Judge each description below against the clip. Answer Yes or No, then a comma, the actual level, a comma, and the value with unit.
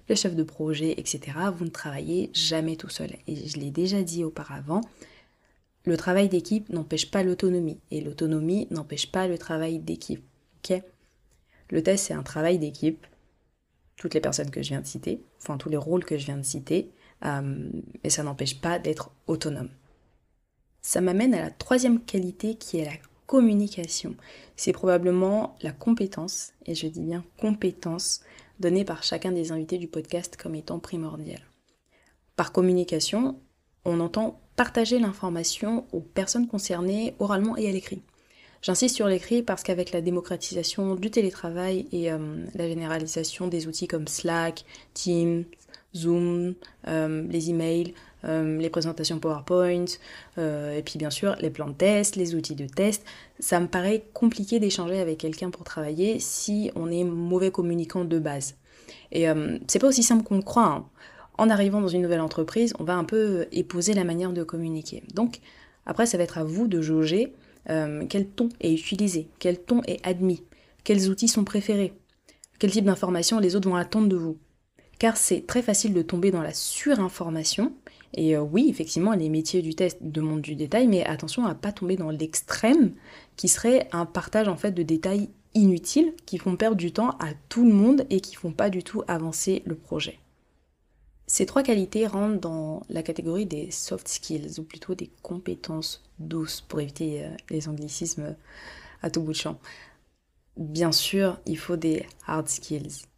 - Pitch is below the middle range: No, medium, 175 Hz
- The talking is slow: No, average, 175 wpm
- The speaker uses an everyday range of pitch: Yes, average, 3.8 semitones